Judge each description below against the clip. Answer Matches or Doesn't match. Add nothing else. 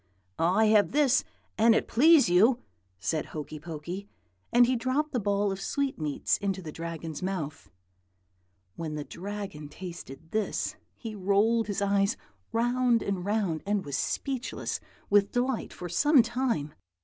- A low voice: Doesn't match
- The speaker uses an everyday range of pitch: Doesn't match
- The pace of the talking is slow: Doesn't match